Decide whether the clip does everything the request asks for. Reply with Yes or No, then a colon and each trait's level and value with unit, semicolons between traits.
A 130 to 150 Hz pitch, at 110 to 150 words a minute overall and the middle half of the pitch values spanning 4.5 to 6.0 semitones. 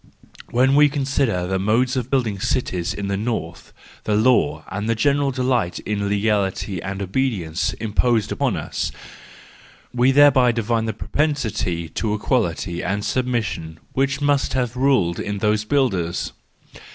No: low, 110 Hz; average, 140 wpm; average, 4.8 semitones